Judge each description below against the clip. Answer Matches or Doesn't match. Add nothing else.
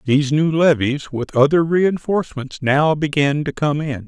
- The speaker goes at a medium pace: Matches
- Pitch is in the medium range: Matches